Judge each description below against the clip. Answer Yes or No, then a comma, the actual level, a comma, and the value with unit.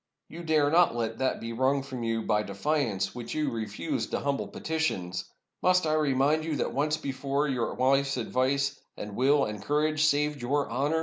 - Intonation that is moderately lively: Yes, average, 4.4 semitones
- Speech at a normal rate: Yes, average, 190 wpm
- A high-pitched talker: No, medium, 140 Hz